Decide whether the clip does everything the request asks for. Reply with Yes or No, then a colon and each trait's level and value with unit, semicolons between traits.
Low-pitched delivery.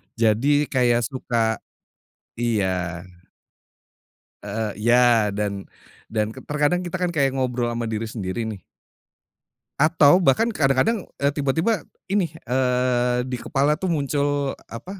Yes: low, 125 Hz